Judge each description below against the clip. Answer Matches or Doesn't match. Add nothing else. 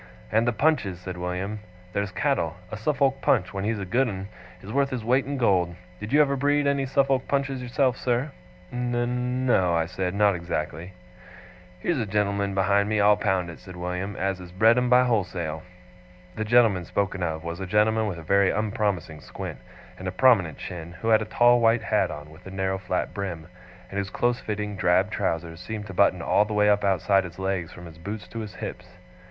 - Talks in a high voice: Doesn't match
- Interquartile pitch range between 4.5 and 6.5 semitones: Matches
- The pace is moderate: Doesn't match